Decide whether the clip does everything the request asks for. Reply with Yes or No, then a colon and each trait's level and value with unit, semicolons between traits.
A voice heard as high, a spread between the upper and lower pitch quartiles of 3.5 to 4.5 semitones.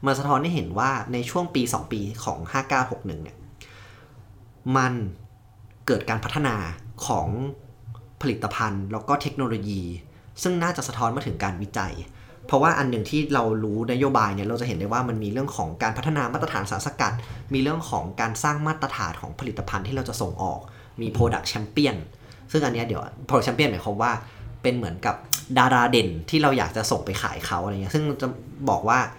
No: low, 115 Hz; average, 4.1 semitones